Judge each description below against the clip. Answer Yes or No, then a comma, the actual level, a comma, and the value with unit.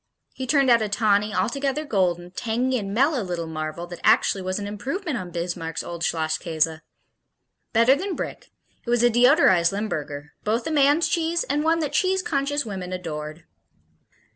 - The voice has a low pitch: No, high, 215 Hz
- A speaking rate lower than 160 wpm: No, average, 165 wpm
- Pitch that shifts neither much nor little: No, wide, 8.1 semitones